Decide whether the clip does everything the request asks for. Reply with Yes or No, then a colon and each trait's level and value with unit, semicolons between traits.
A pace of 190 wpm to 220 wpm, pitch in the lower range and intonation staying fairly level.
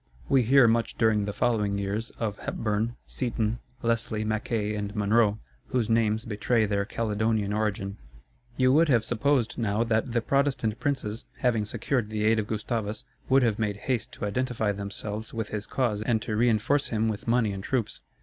No: average, 175 wpm; low, 110 Hz; narrow, 2.2 semitones